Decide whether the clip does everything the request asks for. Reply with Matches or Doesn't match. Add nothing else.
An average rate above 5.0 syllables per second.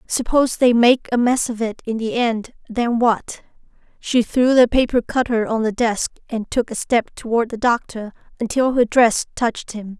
Doesn't match